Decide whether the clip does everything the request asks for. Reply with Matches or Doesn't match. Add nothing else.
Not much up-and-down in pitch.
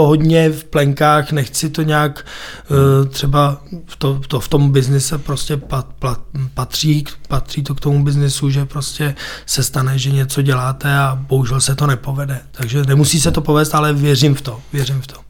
Matches